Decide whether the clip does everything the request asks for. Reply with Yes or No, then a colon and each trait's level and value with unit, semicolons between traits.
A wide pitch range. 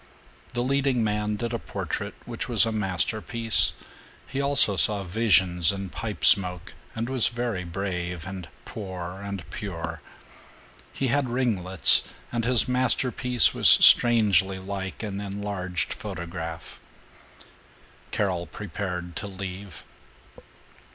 No: average, 4.2 semitones